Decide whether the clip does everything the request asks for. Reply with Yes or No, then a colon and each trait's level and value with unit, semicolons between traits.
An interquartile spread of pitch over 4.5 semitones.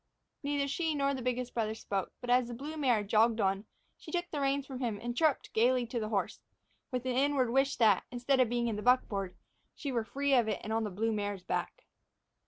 No: average, 3.8 semitones